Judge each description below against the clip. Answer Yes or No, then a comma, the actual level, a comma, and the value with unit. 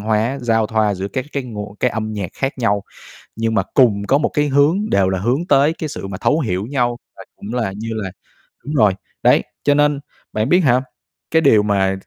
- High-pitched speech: No, low, 115 Hz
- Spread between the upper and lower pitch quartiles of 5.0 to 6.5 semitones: Yes, average, 5.3 semitones